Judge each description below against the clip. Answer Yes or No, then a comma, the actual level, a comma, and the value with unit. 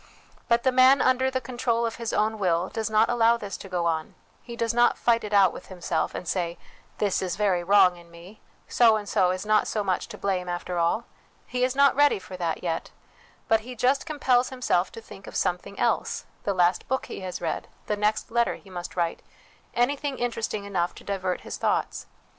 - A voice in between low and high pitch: No, high, 210 Hz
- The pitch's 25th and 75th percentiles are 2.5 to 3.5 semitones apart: No, average, 4.8 semitones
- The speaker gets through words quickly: Yes, fast, 215 wpm